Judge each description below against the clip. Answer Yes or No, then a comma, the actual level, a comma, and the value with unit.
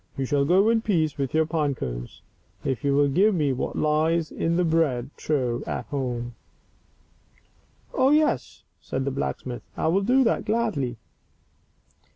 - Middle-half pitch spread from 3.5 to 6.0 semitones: Yes, average, 5.2 semitones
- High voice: No, medium, 150 Hz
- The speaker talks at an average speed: Yes, average, 170 wpm